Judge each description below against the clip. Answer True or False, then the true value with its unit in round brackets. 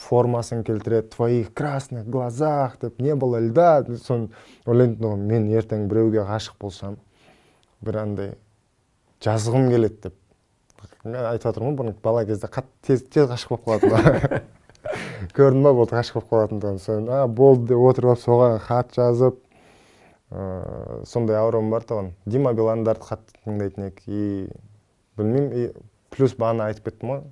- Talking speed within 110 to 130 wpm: False (150 wpm)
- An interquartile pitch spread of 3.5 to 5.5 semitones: False (2.6 semitones)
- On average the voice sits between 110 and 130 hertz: True (115 Hz)